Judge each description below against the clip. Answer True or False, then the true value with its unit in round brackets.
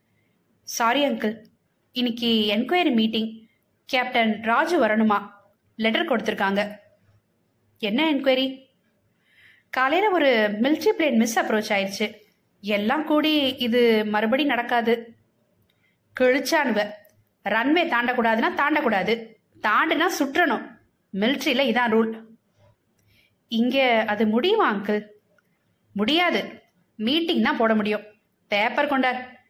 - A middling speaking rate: True (90 wpm)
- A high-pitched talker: True (235 Hz)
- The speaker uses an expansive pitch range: False (4.3 semitones)